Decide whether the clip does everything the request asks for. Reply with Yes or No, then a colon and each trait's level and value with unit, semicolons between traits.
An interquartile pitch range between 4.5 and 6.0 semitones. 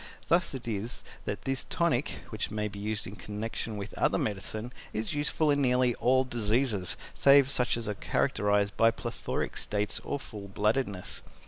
No: average, 4.0 semitones